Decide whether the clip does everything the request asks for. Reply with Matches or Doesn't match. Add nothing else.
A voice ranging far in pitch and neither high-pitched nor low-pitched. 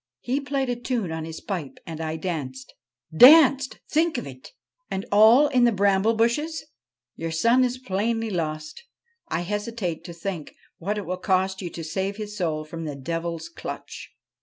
Doesn't match